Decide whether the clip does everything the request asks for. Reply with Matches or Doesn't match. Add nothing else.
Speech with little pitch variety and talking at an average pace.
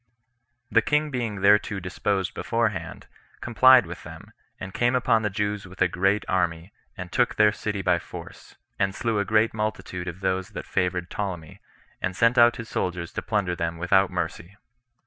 Doesn't match